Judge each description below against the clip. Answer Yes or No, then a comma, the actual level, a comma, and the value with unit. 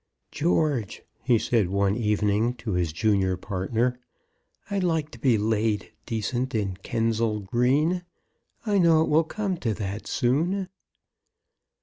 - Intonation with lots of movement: Yes, wide, 6.6 semitones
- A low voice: Yes, low, 115 Hz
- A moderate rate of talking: No, slow, 130 wpm